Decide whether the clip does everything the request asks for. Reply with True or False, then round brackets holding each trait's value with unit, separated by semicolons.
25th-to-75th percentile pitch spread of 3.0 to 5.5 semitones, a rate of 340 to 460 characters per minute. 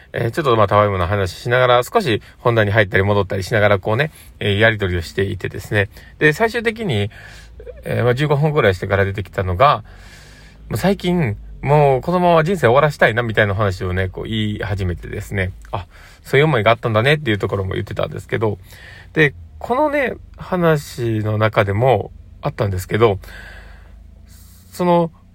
True (5.2 semitones; 370 characters per minute)